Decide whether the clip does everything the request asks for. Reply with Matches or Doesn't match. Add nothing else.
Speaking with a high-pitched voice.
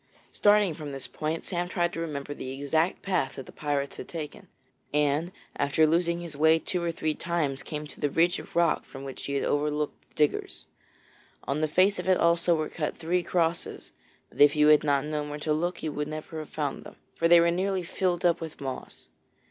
Doesn't match